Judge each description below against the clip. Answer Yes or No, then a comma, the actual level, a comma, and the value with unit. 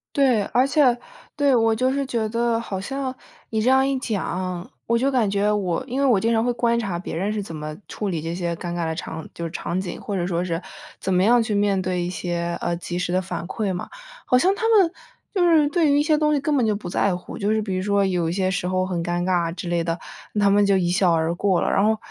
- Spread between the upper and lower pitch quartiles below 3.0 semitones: No, wide, 5.5 semitones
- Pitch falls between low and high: No, high, 200 Hz